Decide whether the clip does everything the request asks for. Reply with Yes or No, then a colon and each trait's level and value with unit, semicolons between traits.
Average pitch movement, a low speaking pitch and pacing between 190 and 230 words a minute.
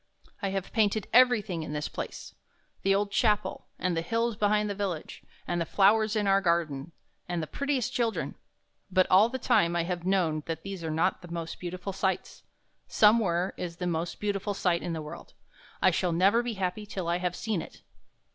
No: average, 3.5 semitones; high, 190 Hz; fast, 205 wpm